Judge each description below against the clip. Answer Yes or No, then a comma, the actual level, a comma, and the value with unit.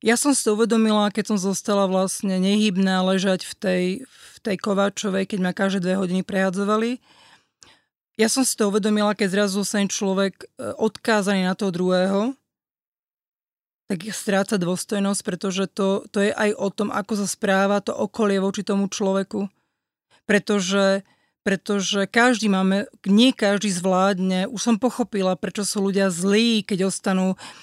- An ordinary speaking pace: Yes, average, 155 wpm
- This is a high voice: Yes, high, 200 Hz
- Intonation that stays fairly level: Yes, narrow, 1.7 semitones